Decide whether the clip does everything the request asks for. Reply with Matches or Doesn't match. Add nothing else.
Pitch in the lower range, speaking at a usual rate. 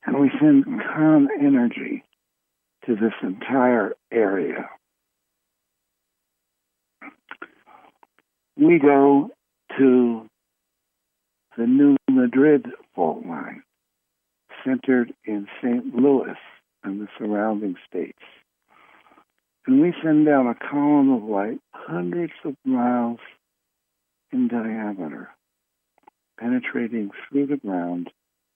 Doesn't match